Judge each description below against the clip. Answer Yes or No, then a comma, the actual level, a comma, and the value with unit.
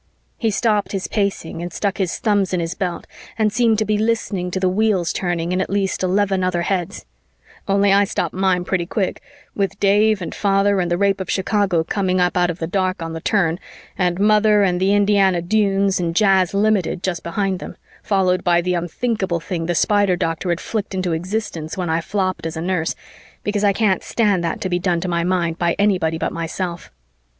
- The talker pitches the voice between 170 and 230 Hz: Yes, high, 190 Hz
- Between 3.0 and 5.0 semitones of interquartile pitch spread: No, narrow, 2.5 semitones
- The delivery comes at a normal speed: No, fast, 210 wpm